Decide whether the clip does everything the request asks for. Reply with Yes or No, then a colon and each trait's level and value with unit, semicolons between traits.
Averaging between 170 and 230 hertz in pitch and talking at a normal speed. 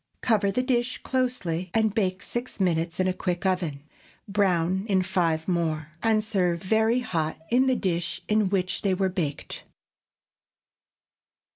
Yes: high, 190 Hz; average, 145 wpm